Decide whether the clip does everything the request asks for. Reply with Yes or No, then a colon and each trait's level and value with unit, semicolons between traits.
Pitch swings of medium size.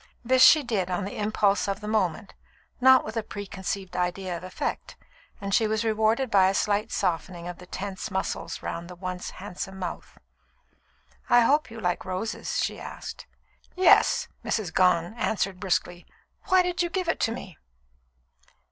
Yes: average, 3.5 semitones